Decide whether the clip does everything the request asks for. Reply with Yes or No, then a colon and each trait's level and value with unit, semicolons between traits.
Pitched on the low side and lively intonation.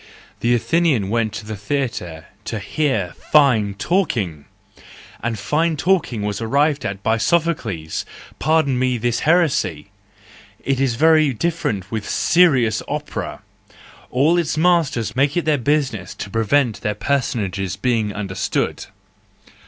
Yes: low, 120 Hz; wide, 6.4 semitones